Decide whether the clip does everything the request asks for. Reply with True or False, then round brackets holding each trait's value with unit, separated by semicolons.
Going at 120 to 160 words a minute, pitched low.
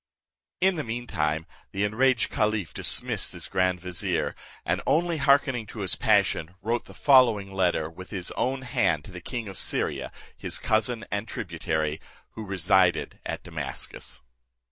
True (155 wpm; 100 Hz)